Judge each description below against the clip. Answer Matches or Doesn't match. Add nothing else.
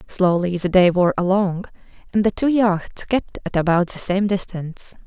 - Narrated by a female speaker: Matches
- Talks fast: Doesn't match